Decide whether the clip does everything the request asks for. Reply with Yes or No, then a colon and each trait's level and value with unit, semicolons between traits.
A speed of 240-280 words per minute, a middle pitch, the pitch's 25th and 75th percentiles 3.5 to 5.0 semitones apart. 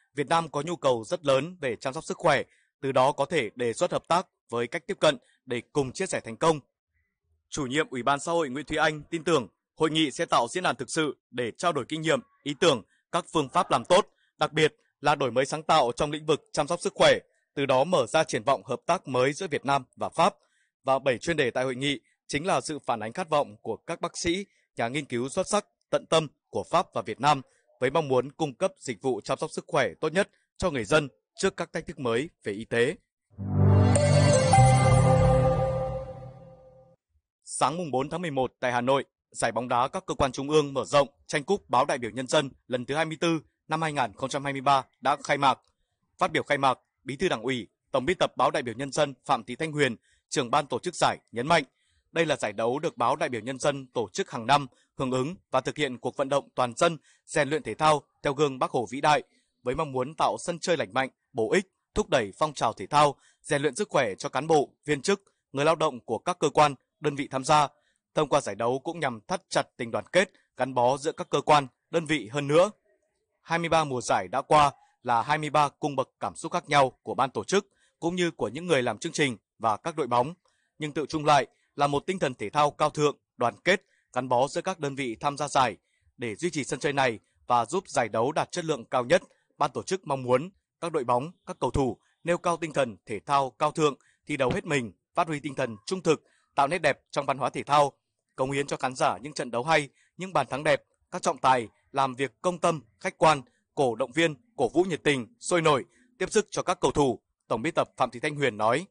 Yes: average, 245 wpm; medium, 145 Hz; average, 4.2 semitones